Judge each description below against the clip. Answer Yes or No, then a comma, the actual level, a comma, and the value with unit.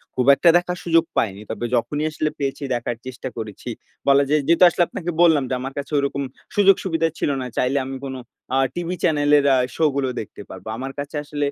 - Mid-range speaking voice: Yes, medium, 145 Hz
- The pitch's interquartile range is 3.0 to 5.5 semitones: Yes, average, 3.9 semitones